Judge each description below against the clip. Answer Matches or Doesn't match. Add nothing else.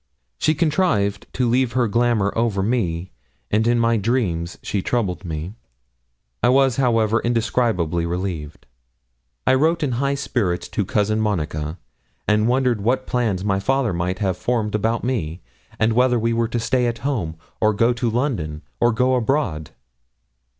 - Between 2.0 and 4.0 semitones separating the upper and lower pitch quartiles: Doesn't match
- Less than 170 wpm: Matches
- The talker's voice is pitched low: Matches